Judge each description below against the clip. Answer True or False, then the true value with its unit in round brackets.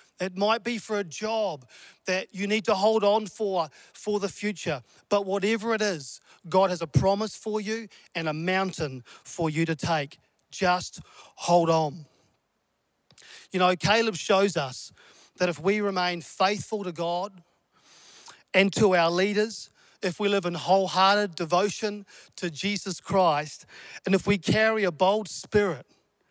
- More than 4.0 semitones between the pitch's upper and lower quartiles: False (3.5 semitones)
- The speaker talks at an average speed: True (155 wpm)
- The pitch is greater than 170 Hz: True (190 Hz)